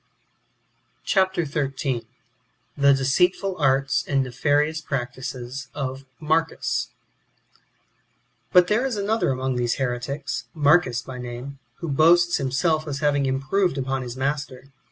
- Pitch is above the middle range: No, medium, 140 Hz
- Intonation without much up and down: No, average, 3.3 semitones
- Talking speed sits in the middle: No, slow, 130 wpm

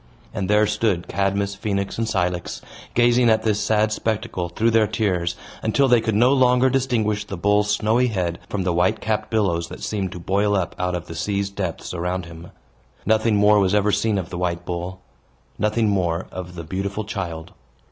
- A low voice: Yes, low, 100 Hz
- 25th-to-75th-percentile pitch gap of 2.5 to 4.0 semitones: Yes, average, 3.3 semitones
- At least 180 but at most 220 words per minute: Yes, average, 190 wpm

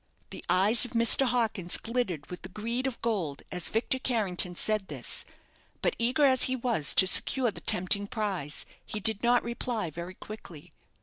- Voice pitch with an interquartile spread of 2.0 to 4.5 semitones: No, average, 5.0 semitones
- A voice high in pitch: Yes, high, 215 Hz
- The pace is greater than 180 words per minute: No, average, 175 wpm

